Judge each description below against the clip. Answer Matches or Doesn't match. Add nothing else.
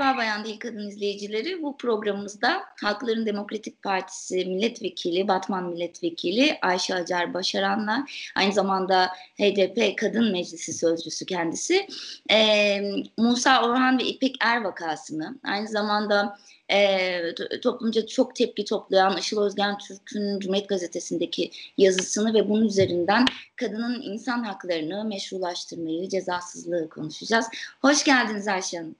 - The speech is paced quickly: Doesn't match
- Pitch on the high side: Matches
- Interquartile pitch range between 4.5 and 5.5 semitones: Doesn't match